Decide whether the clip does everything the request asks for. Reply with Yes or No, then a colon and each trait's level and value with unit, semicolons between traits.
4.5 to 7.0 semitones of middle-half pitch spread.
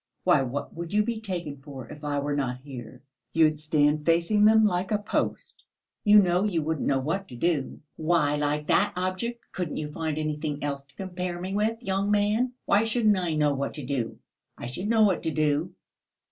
Yes: wide, 5.4 semitones